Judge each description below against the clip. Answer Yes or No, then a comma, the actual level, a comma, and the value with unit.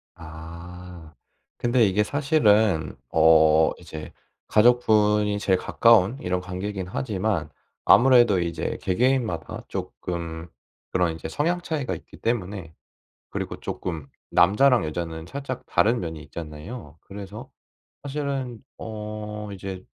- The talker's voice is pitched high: No, low, 100 Hz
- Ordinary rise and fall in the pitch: No, wide, 5.7 semitones